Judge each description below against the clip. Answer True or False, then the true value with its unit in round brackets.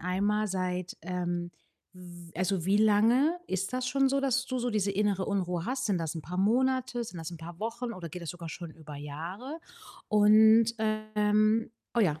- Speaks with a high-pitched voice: True (205 Hz)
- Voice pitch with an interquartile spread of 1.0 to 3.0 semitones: False (4.5 semitones)